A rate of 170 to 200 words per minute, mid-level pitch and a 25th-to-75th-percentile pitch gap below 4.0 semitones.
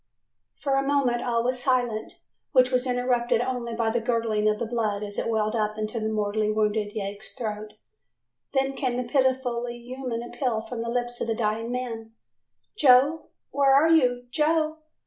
No: average, 180 wpm; high, 240 Hz; average, 2.7 semitones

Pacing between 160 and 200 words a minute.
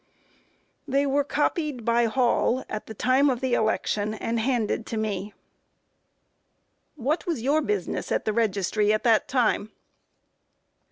No: average, 150 wpm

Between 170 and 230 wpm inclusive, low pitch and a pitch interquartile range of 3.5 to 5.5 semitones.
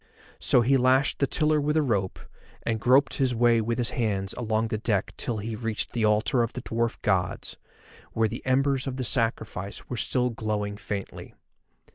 No: average, 185 wpm; low, 115 Hz; average, 3.1 semitones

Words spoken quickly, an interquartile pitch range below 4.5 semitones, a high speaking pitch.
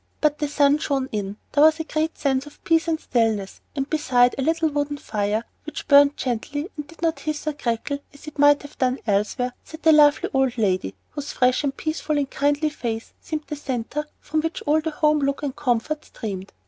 Yes: fast, 210 wpm; average, 3.5 semitones; very high, 285 Hz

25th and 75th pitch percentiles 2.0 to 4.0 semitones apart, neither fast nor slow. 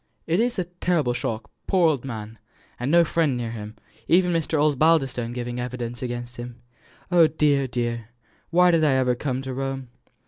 No: average, 5.0 semitones; average, 175 wpm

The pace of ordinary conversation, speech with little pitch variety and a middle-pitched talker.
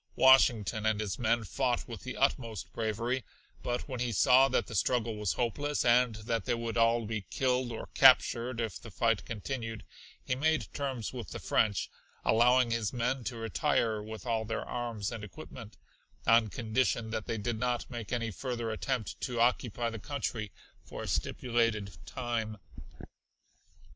No: average, 165 wpm; narrow, 2.2 semitones; low, 115 Hz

